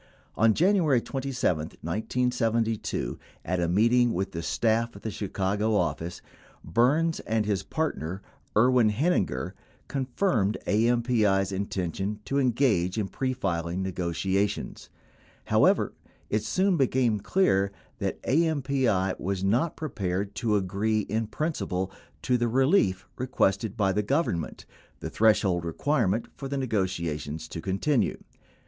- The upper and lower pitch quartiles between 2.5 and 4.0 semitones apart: No, average, 5.1 semitones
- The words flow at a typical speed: No, slow, 125 wpm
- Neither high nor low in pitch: No, low, 110 Hz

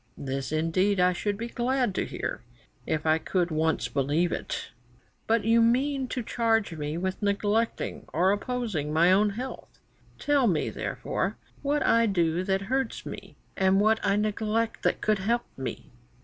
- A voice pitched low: No, high, 200 Hz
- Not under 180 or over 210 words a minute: No, average, 165 wpm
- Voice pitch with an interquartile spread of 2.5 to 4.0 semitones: No, average, 5.2 semitones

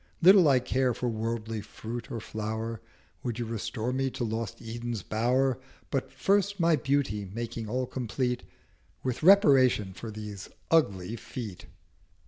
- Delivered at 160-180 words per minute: No, average, 140 wpm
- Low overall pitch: Yes, low, 120 Hz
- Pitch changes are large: No, average, 3.3 semitones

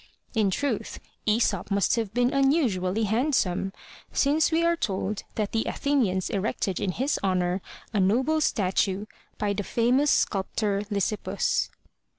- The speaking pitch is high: Yes, high, 215 Hz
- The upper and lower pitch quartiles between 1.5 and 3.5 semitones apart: No, wide, 5.4 semitones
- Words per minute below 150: Yes, average, 140 wpm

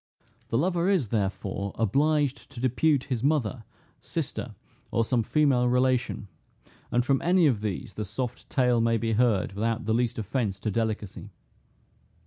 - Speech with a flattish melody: No, average, 3.5 semitones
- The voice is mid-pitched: No, low, 120 Hz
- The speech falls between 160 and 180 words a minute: No, average, 150 wpm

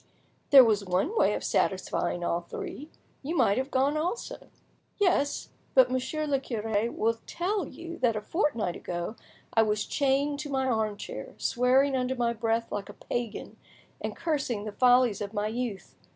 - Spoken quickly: No, average, 165 wpm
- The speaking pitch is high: Yes, very high, 250 Hz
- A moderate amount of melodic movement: Yes, average, 4.8 semitones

